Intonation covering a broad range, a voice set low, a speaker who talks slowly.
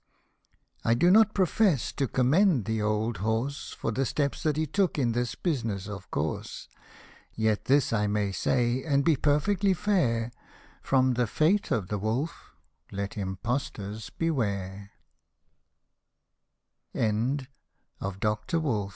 Yes: wide, 6.0 semitones; low, 125 Hz; slow, 115 wpm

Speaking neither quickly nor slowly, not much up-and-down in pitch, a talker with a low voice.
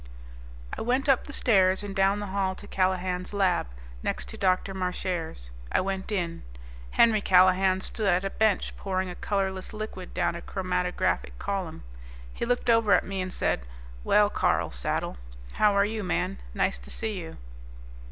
No: average, 170 wpm; narrow, 2.1 semitones; high, 190 Hz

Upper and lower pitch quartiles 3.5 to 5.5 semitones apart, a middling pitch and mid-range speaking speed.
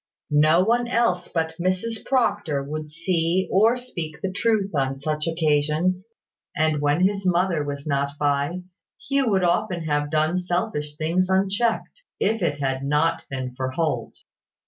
Yes: average, 4.3 semitones; medium, 165 Hz; average, 150 wpm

